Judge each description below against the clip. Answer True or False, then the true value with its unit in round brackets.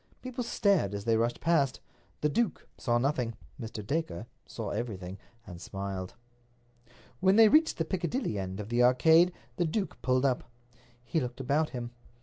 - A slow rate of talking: False (165 wpm)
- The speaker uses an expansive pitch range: True (6.9 semitones)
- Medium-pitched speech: False (125 Hz)